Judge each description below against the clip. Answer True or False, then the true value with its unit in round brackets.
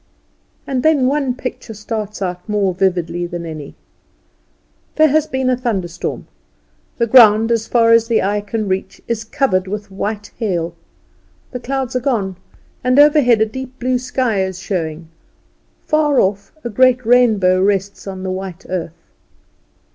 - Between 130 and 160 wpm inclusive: True (155 wpm)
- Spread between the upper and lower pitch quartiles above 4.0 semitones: True (5.1 semitones)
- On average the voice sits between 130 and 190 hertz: False (215 Hz)